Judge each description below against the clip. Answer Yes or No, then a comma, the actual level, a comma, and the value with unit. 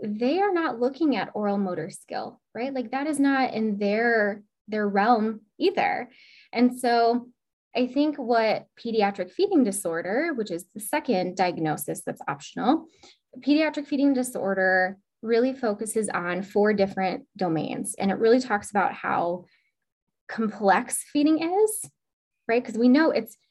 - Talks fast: No, average, 145 wpm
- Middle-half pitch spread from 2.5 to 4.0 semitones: No, average, 5.0 semitones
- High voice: Yes, high, 230 Hz